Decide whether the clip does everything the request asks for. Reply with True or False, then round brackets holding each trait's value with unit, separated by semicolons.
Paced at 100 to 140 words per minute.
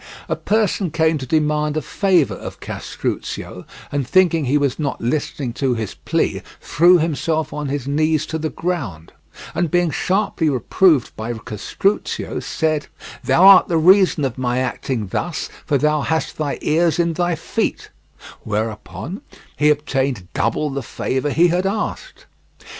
False (155 wpm)